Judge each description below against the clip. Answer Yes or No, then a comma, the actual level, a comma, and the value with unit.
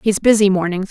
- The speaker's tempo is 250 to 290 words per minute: No, average, 200 wpm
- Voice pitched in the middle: No, high, 195 Hz